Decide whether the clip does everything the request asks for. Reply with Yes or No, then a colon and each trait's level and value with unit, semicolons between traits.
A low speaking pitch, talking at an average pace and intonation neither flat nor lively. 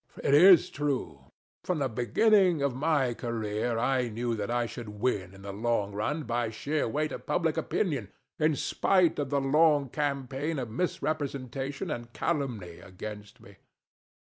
Yes: low, 130 Hz; average, 165 wpm; average, 4.6 semitones